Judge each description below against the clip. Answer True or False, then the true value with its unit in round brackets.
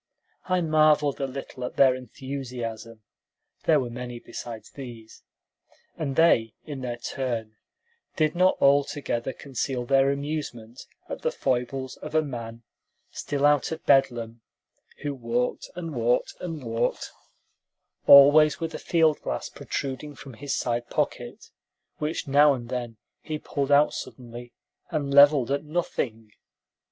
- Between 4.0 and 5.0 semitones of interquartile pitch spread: False (3.5 semitones)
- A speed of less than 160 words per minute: True (135 wpm)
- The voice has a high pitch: False (135 Hz)